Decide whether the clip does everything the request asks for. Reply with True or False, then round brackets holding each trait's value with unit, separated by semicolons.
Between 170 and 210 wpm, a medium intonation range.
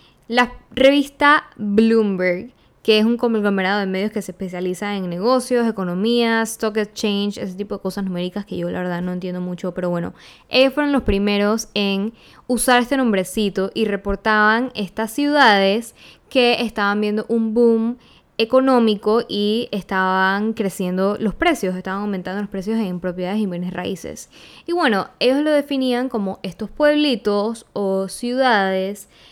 False (150 wpm; 3.6 semitones)